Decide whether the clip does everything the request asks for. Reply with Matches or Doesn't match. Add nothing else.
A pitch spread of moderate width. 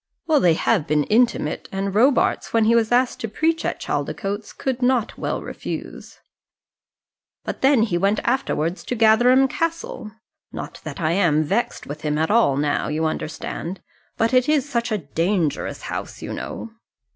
Doesn't match